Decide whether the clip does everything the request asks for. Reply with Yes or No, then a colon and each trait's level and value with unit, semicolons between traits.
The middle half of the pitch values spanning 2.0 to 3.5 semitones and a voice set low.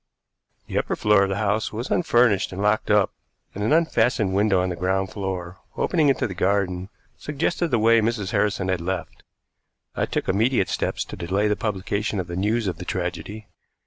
Yes: average, 2.9 semitones; low, 100 Hz